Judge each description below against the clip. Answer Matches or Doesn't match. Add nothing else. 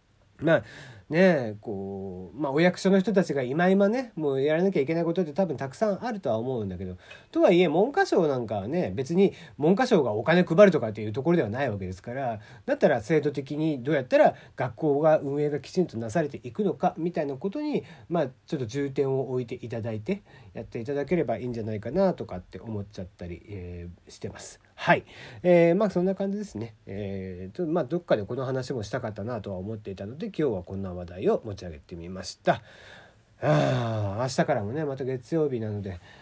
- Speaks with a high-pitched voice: Doesn't match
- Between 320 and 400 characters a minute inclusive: Doesn't match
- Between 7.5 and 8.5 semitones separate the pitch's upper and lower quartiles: Matches